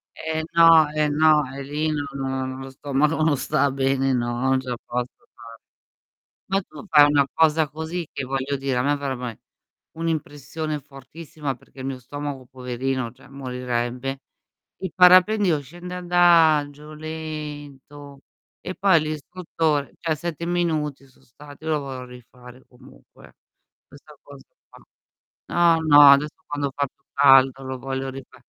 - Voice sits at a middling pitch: Yes, medium, 145 Hz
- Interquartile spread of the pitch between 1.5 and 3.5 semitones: Yes, average, 3.0 semitones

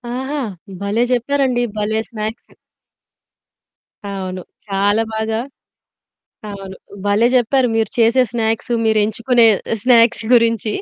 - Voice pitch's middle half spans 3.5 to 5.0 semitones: No, narrow, 2.5 semitones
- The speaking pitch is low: No, high, 225 Hz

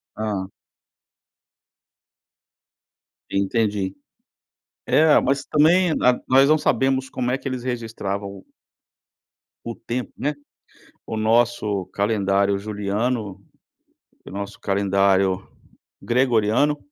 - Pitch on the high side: No, low, 110 Hz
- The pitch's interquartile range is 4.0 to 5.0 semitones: Yes, average, 4.4 semitones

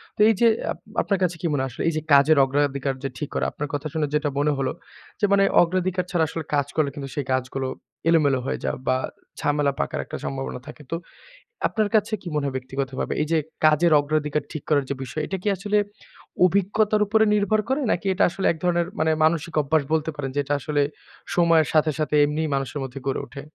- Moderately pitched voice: Yes, medium, 155 Hz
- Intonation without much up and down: No, average, 3.8 semitones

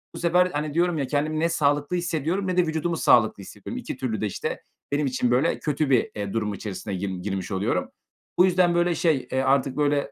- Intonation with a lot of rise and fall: Yes, wide, 6.0 semitones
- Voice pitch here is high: No, medium, 145 Hz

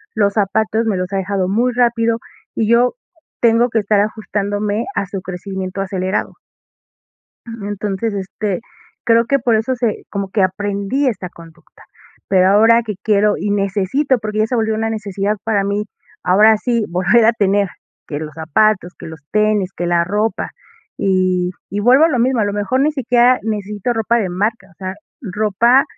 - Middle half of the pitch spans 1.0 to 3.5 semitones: Yes, average, 2.9 semitones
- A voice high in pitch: Yes, high, 210 Hz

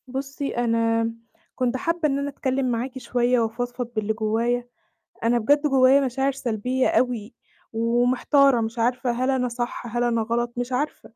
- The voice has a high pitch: Yes, high, 245 Hz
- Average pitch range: No, narrow, 2.1 semitones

